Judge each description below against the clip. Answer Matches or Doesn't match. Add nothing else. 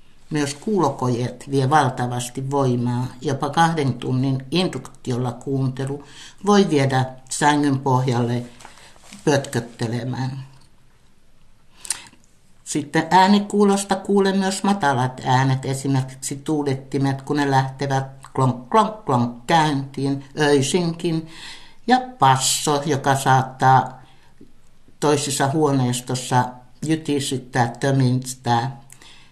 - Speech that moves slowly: Matches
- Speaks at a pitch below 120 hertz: Doesn't match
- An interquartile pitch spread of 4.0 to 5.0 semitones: Doesn't match